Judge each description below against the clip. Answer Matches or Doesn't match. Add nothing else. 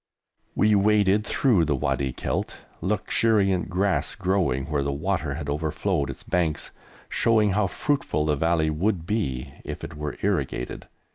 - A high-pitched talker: Doesn't match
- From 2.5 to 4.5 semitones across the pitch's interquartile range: Doesn't match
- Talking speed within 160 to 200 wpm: Doesn't match